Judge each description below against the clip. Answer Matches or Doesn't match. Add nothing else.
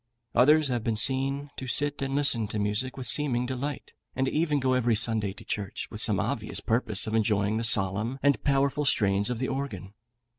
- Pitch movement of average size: Matches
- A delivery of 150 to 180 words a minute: Doesn't match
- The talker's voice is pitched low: Matches